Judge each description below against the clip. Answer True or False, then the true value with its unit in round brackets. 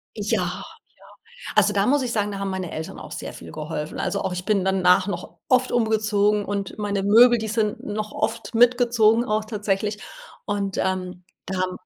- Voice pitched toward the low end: False (205 Hz)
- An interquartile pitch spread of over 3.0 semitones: False (2.6 semitones)